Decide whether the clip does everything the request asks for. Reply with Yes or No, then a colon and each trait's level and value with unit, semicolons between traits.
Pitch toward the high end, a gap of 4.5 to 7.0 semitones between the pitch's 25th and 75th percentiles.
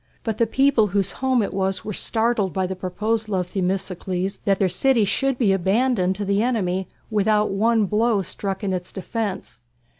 No: high, 200 Hz; average, 3.0 semitones